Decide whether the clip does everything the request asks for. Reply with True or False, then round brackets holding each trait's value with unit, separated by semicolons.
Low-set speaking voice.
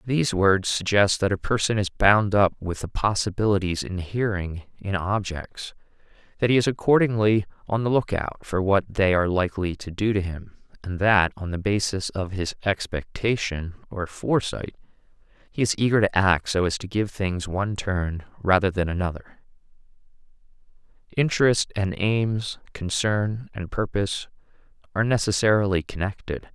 True (100 Hz)